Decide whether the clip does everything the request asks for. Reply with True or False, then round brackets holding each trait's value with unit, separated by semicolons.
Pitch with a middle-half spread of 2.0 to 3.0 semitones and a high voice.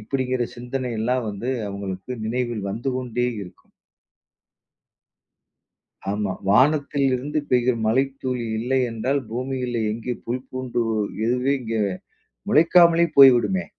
False (2.6 semitones; 125 Hz)